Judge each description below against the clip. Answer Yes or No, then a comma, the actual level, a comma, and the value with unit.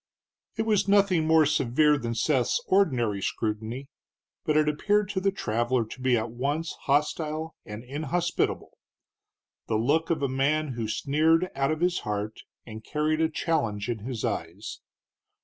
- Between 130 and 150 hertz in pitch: Yes, medium, 140 Hz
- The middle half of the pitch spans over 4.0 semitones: Yes, wide, 5.6 semitones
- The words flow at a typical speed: Yes, average, 155 wpm